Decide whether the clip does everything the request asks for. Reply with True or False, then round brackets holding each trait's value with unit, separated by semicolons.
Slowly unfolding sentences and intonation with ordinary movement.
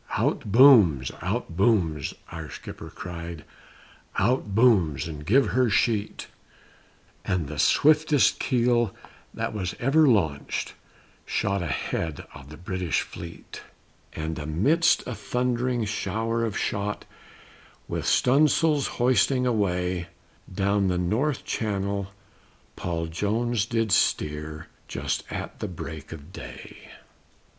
False (115 wpm; 6.3 semitones)